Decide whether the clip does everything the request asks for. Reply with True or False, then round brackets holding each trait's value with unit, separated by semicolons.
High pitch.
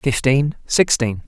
False (135 Hz)